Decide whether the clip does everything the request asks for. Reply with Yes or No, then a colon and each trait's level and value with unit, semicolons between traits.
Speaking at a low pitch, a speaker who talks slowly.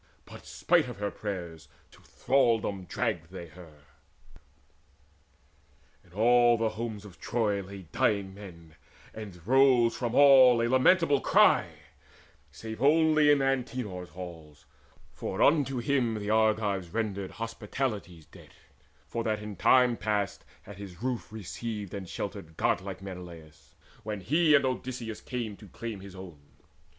Yes: low, 105 Hz; slow, 130 wpm